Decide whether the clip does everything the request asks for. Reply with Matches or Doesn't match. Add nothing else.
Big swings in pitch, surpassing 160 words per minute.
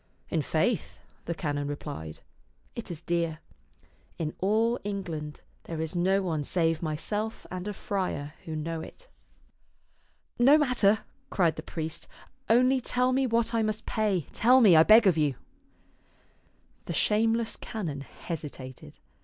Doesn't match